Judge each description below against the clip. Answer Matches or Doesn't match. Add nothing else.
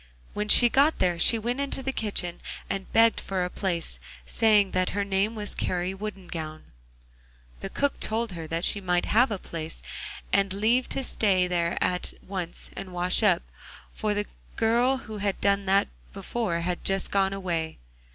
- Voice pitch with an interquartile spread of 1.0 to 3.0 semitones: Doesn't match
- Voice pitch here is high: Matches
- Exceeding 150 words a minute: Matches